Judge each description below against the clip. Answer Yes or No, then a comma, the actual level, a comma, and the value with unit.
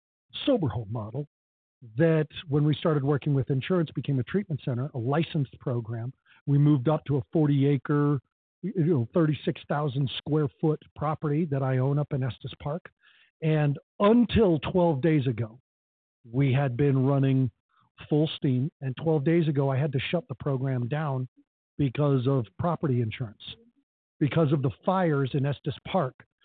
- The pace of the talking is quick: No, average, 155 wpm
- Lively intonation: No, average, 3.1 semitones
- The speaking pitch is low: No, medium, 145 Hz